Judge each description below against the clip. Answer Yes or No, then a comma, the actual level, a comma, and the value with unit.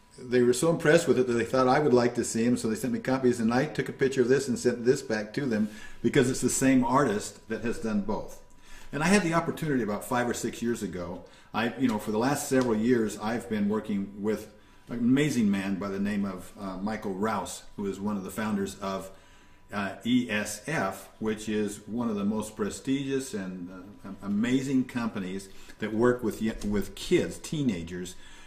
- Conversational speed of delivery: No, fast, 215 wpm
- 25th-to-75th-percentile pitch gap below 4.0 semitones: No, average, 4.3 semitones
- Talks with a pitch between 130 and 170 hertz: No, low, 115 Hz